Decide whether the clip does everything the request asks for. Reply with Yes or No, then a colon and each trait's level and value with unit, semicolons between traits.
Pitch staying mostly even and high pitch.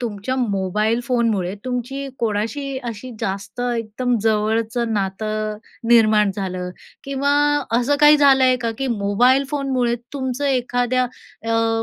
No: average, 3.3 semitones; high, 235 Hz